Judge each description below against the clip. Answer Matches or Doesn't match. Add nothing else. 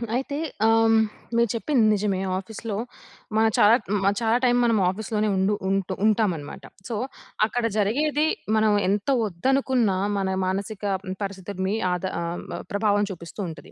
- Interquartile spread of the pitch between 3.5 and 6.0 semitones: Doesn't match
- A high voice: Matches